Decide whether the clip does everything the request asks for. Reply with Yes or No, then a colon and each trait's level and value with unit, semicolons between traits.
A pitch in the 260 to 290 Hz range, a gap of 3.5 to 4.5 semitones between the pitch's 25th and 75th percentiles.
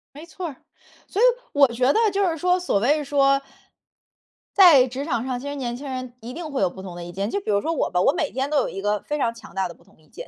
No: very high, 270 Hz; average, 5.1 semitones